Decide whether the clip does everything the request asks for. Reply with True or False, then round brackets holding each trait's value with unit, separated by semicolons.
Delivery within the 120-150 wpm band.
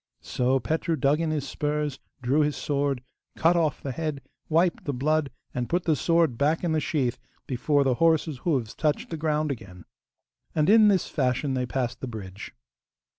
False (180 wpm)